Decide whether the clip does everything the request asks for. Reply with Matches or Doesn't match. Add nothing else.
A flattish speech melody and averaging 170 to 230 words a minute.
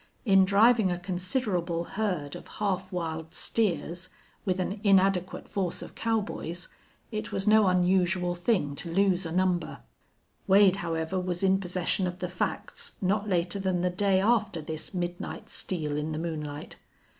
Doesn't match